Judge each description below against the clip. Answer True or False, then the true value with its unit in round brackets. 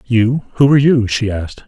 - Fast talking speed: False (180 wpm)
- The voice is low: True (120 Hz)